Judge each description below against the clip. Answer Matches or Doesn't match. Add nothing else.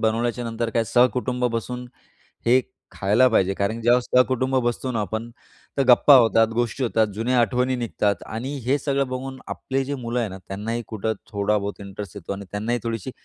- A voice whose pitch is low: Matches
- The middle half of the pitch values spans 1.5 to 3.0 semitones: Matches